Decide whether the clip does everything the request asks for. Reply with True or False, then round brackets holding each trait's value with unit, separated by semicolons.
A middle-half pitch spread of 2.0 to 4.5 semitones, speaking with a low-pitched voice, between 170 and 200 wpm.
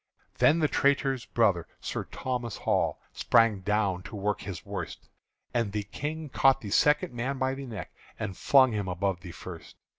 False (5.4 semitones; 115 Hz; 175 wpm)